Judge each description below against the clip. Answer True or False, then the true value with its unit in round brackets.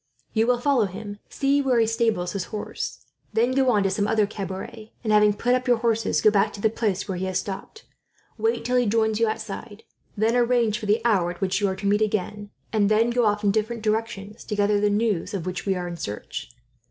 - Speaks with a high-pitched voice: True (215 Hz)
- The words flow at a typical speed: False (240 wpm)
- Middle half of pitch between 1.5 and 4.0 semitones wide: True (2.4 semitones)